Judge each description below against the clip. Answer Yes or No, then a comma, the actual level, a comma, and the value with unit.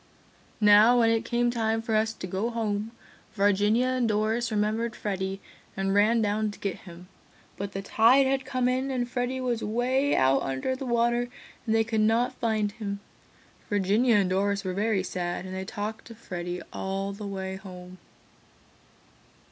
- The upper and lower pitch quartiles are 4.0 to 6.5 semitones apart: No, average, 3.4 semitones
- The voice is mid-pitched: No, high, 215 Hz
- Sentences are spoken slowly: No, average, 170 wpm